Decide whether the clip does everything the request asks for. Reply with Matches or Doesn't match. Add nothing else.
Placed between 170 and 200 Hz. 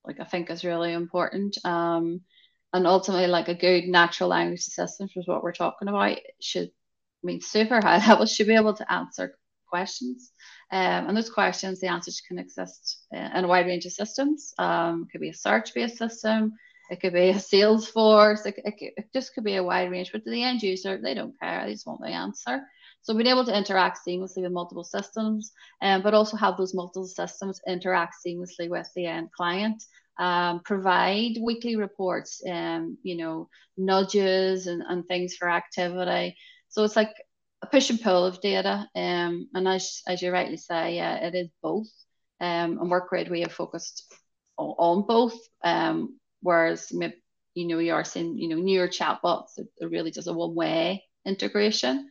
Matches